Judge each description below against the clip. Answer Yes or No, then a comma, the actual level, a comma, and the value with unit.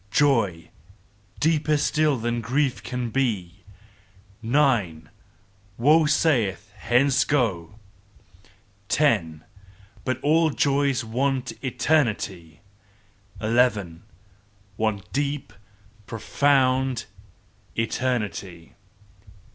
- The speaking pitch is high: No, low, 120 Hz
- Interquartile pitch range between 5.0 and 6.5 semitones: Yes, wide, 5.4 semitones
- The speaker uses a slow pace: Yes, slow, 75 wpm